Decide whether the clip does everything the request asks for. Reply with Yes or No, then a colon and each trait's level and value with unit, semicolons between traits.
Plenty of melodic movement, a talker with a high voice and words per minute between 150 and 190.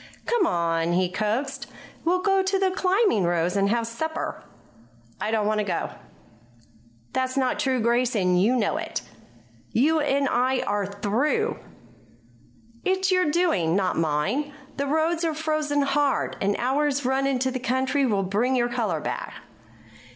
Yes: wide, 6.6 semitones; very high, 255 Hz; average, 160 wpm